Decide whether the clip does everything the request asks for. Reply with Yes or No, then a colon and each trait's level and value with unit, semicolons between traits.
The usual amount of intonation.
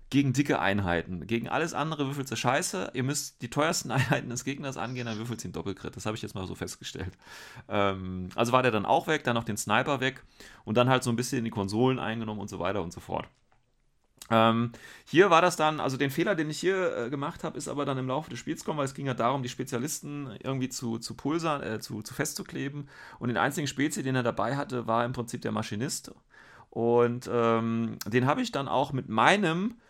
Yes: average, 3.8 semitones